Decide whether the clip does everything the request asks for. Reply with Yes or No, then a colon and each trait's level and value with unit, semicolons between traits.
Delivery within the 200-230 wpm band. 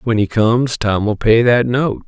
Yes: fast, 205 wpm